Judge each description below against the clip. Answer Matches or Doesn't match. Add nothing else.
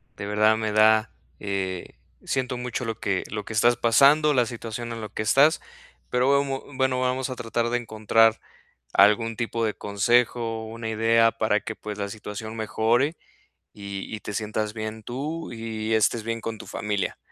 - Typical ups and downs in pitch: Doesn't match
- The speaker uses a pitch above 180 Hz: Doesn't match